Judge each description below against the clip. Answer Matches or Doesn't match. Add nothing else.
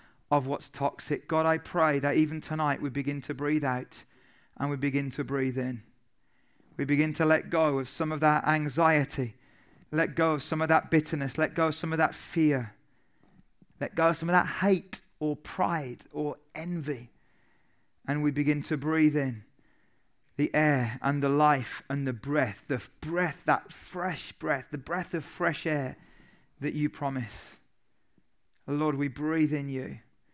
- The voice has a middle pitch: Matches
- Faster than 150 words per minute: Matches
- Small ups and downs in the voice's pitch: Matches